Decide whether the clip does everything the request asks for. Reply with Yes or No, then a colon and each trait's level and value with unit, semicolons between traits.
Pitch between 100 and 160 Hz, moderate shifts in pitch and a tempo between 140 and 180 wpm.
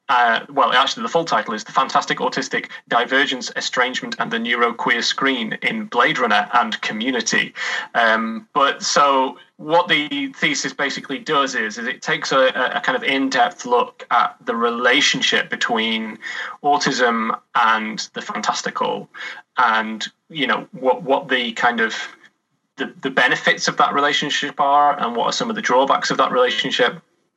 No: medium, 140 Hz; wide, 6.7 semitones; average, 160 wpm